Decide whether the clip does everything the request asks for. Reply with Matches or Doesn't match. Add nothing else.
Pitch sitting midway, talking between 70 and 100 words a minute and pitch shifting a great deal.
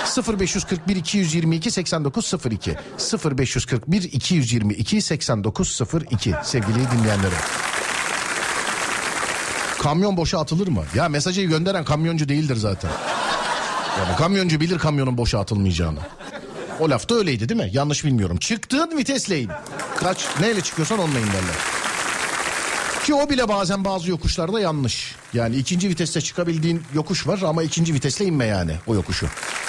Doesn't match